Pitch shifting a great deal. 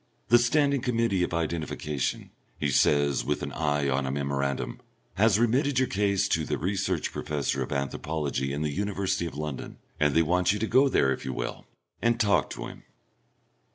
Yes: wide, 6.5 semitones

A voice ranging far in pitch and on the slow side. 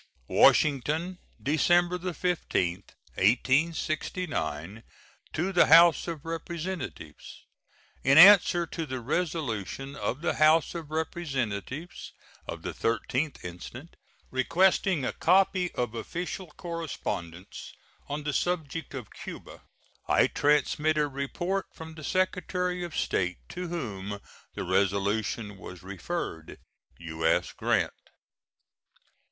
Yes: wide, 7.6 semitones; slow, 105 wpm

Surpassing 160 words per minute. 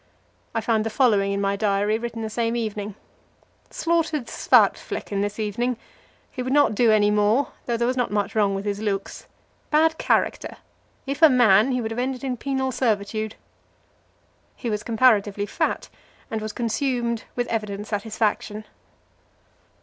No: average, 155 wpm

